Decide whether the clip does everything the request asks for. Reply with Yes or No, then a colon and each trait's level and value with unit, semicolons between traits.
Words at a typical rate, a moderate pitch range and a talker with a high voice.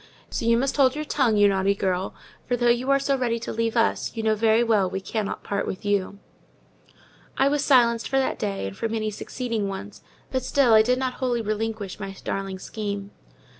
No: fast, 210 wpm; average, 3.7 semitones; high, 225 Hz